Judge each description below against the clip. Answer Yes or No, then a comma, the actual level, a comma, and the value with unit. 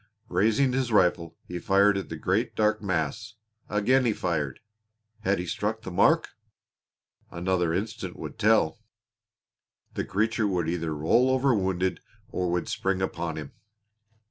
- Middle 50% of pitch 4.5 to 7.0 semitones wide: No, average, 3.9 semitones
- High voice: No, very low, 95 Hz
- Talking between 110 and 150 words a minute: Yes, average, 145 wpm